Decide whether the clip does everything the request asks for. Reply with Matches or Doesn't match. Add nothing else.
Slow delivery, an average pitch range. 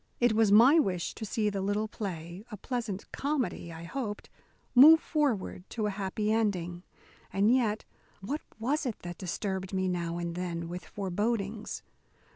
Doesn't match